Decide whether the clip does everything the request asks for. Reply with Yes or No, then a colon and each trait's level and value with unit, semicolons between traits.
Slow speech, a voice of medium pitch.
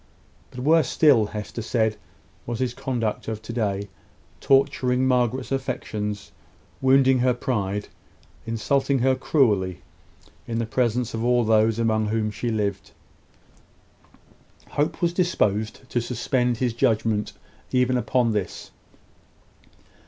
No: slow, 120 wpm; low, 120 Hz